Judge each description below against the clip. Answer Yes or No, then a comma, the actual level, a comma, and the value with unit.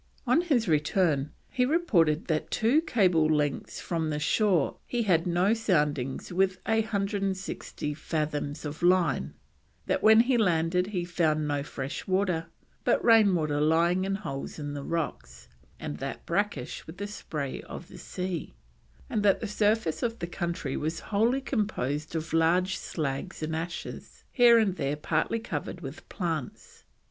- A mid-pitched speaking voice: Yes, medium, 175 Hz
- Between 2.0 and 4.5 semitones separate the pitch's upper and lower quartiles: No, average, 5.3 semitones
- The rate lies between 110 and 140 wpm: No, average, 160 wpm